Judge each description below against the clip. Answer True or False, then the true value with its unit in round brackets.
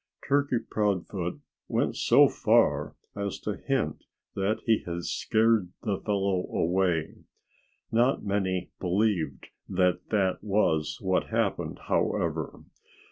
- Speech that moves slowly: True (110 wpm)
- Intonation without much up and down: False (3.1 semitones)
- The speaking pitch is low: True (95 Hz)